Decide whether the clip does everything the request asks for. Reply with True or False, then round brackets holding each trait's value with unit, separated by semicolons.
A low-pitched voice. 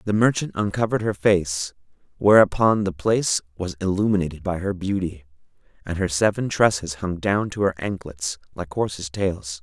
True (95 Hz)